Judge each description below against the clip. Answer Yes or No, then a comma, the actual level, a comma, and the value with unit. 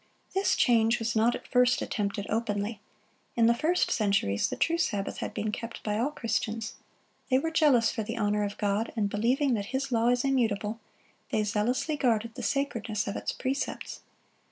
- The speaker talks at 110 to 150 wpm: No, average, 180 wpm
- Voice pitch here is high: Yes, high, 230 Hz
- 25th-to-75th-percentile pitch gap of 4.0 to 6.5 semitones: No, average, 3.5 semitones